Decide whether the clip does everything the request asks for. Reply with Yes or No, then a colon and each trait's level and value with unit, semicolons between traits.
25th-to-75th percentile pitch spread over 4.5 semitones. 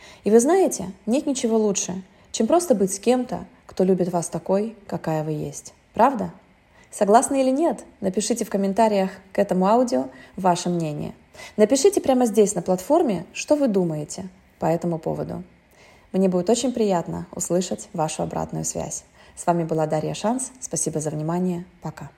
Yes: average, 5.2 semitones